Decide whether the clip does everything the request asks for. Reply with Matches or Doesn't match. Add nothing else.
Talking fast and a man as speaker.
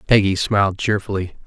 Doesn't match